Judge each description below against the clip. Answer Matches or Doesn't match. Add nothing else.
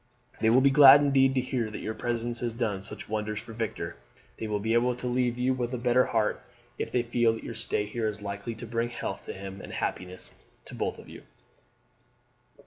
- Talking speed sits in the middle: Doesn't match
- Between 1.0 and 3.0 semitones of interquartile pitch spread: Matches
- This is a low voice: Matches